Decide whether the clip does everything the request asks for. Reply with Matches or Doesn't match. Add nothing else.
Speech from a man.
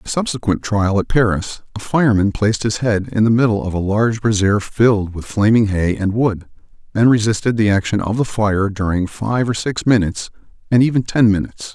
Matches